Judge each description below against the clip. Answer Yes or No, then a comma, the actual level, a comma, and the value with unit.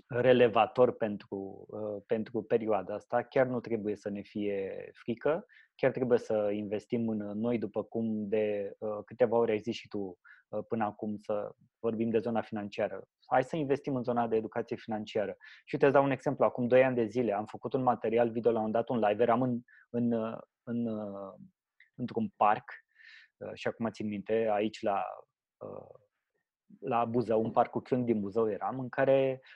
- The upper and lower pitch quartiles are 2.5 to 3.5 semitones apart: Yes, average, 2.9 semitones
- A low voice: Yes, low, 115 Hz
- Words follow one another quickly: Yes, fast, 180 wpm